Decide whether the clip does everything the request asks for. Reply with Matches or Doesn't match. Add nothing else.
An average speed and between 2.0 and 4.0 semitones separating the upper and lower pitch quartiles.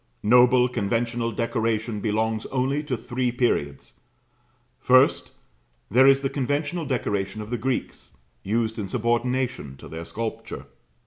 Doesn't match